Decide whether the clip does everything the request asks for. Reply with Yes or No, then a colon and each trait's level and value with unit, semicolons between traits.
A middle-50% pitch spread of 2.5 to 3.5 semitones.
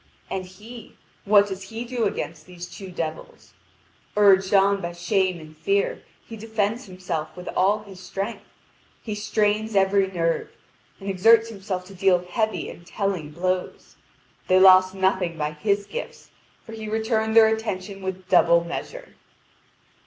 Yes: average, 3.0 semitones